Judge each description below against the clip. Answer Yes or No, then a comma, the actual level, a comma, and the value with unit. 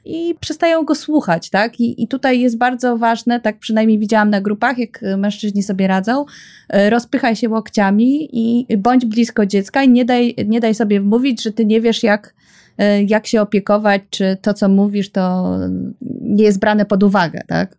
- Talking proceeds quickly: Yes, fast, 180 wpm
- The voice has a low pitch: No, high, 220 Hz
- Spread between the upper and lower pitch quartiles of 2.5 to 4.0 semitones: Yes, average, 2.9 semitones